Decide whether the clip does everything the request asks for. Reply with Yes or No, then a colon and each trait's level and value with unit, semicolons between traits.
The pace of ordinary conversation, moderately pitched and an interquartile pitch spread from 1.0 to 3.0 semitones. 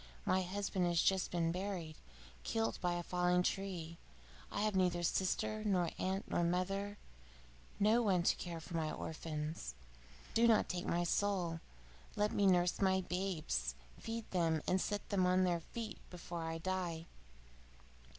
Yes: average, 155 wpm; medium, 180 Hz; narrow, 2.5 semitones